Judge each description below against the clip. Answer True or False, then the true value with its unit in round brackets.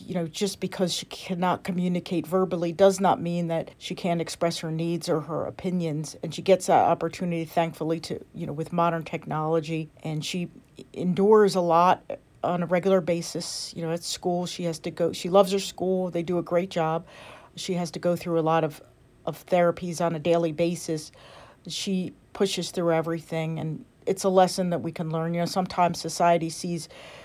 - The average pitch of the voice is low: False (170 Hz)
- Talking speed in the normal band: True (195 wpm)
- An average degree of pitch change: False (1.8 semitones)